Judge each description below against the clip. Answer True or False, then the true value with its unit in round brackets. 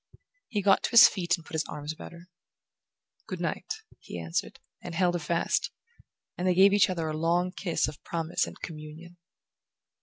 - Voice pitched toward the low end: False (170 Hz)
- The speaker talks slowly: False (185 wpm)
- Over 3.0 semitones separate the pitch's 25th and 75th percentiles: False (2.5 semitones)